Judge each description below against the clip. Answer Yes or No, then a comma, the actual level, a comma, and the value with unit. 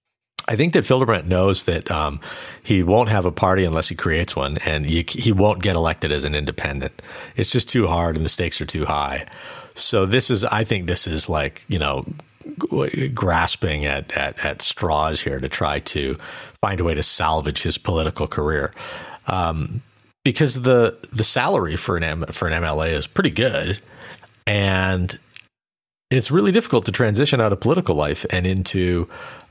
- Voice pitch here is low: Yes, very low, 95 Hz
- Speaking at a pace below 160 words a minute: No, average, 175 wpm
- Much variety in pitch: Yes, wide, 5.9 semitones